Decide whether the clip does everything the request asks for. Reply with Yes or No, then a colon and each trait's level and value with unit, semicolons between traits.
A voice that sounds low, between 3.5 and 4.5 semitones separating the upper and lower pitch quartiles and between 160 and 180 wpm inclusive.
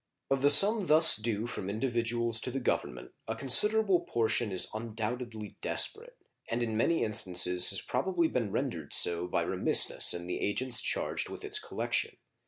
No: low, 120 Hz; average, 5.1 semitones; average, 165 wpm